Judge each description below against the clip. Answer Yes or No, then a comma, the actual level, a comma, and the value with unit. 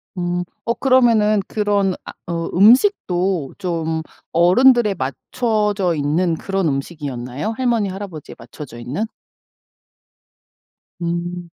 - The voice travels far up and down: No, average, 4.6 semitones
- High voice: No, medium, 180 Hz